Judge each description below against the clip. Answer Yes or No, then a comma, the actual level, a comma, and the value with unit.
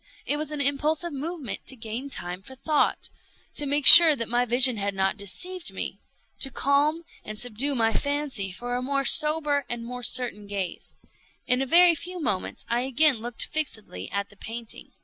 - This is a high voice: Yes, very high, 260 Hz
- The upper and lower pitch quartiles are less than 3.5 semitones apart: No, average, 4.8 semitones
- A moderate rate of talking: Yes, average, 175 wpm